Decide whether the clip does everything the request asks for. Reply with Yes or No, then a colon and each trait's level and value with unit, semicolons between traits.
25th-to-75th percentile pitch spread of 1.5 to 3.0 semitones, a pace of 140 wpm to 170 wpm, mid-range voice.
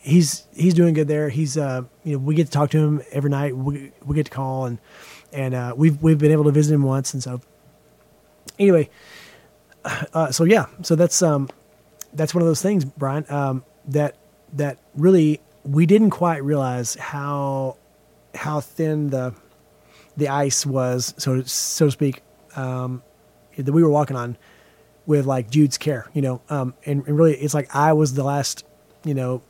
No: narrow, 2.4 semitones; average, 185 wpm; medium, 145 Hz